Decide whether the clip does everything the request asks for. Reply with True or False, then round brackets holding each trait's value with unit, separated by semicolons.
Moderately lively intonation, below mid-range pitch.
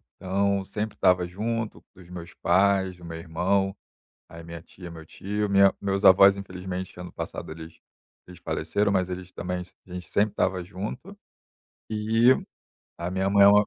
False (2.1 semitones; 95 Hz)